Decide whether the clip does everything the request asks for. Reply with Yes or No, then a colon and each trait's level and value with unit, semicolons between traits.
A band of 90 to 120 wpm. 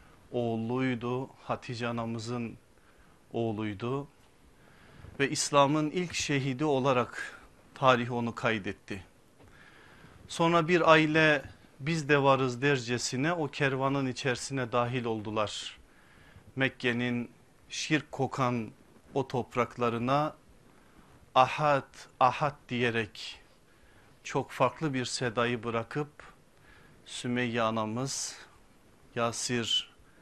No: slow, 80 wpm